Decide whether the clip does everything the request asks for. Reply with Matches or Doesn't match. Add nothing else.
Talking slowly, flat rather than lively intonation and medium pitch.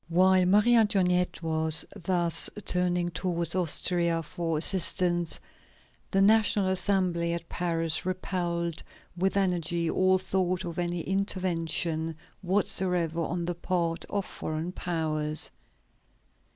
Matches